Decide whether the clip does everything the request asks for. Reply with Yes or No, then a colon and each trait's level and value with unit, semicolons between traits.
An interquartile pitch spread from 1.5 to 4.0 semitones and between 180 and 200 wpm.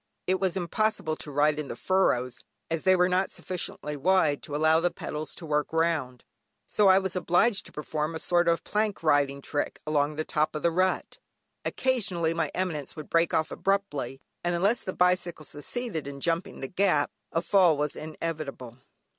Yes: average, 3.7 semitones; average, 185 wpm